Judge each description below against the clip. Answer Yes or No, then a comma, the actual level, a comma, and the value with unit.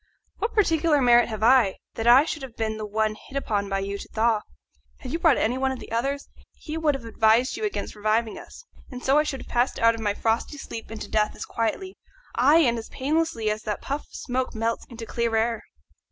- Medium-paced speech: No, fast, 235 wpm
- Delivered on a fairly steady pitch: No, average, 3.8 semitones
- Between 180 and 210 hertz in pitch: No, high, 235 Hz